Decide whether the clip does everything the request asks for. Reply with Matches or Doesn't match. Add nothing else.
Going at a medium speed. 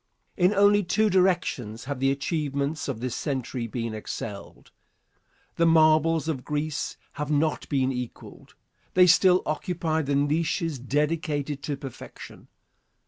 Doesn't match